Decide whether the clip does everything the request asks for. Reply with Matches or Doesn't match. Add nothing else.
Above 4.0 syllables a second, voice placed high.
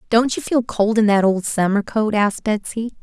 Matches